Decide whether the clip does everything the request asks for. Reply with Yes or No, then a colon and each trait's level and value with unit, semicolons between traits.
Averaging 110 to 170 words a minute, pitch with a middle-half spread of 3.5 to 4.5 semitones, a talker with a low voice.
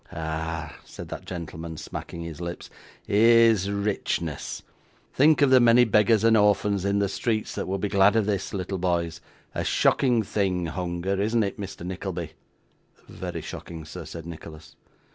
Yes: average, 160 wpm; average, 3.9 semitones; very low, 95 Hz